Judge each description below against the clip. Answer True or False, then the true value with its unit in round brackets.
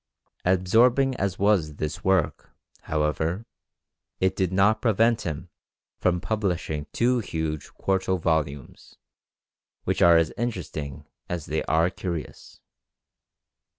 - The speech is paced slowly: True (110 wpm)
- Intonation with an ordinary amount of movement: True (4.1 semitones)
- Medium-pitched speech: False (90 Hz)